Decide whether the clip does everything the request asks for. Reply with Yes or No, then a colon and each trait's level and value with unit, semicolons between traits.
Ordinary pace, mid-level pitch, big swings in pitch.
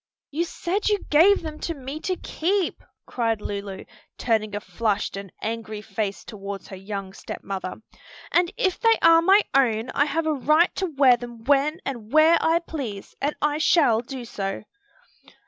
No: average, 175 wpm; very high, 265 Hz; wide, 7.4 semitones